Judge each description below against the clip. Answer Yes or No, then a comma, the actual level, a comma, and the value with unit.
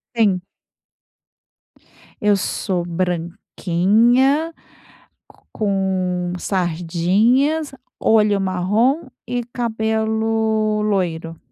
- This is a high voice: Yes, high, 210 Hz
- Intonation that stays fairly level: No, average, 3.7 semitones